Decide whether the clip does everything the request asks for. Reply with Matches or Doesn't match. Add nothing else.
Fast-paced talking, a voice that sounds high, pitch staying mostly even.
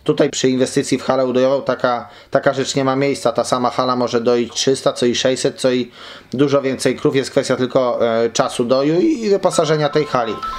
Doesn't match